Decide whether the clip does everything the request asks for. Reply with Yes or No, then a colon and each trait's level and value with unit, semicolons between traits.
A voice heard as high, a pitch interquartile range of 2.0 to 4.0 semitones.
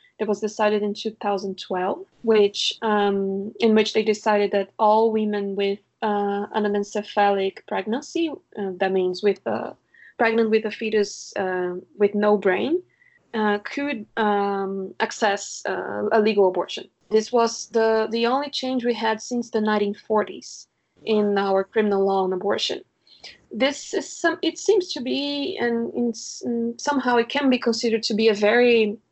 Yes: high, 215 Hz; narrow, 2.6 semitones